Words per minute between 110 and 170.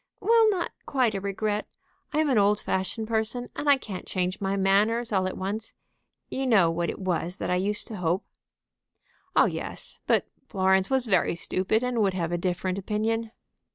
No: average, 190 wpm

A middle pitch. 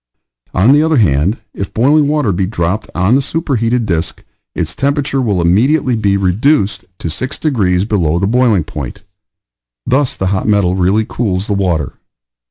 No: low, 105 Hz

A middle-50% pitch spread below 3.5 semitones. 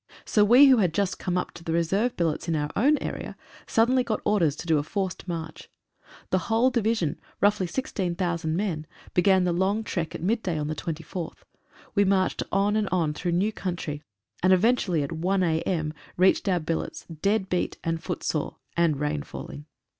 No: average, 3.8 semitones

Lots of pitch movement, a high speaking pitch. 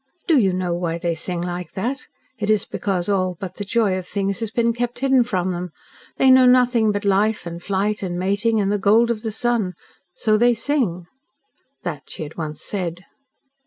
No: average, 4.3 semitones; high, 200 Hz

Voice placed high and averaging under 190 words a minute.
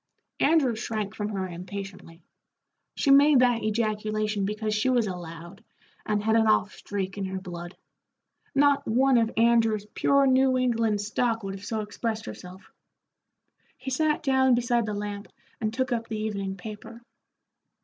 Yes: high, 215 Hz; average, 160 wpm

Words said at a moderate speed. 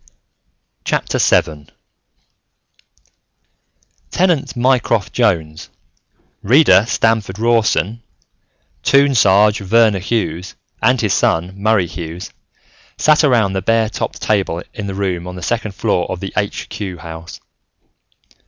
No: slow, 110 wpm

